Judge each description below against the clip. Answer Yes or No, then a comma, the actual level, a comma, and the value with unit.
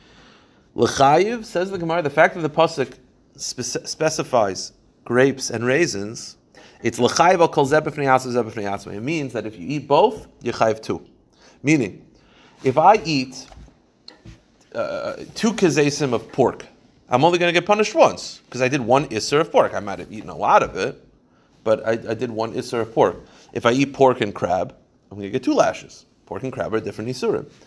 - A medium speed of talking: Yes, average, 185 wpm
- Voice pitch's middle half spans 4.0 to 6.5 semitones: Yes, average, 5.2 semitones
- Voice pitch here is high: No, low, 130 Hz